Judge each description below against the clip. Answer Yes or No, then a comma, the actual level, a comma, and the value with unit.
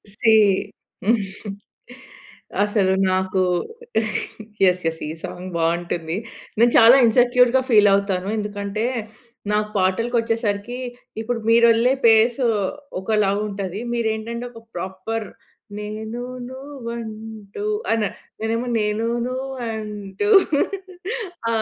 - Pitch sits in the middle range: No, high, 220 Hz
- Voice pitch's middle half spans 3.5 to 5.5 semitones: No, average, 2.9 semitones